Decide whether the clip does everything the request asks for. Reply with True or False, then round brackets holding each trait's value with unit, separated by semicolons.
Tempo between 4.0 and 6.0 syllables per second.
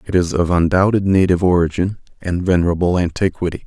False (6.3 syllables/s)